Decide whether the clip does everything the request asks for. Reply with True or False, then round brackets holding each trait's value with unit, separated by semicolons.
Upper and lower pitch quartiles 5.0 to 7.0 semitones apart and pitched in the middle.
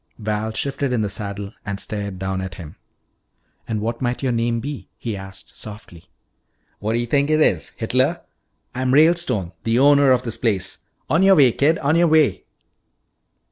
False (5.6 semitones; 115 Hz)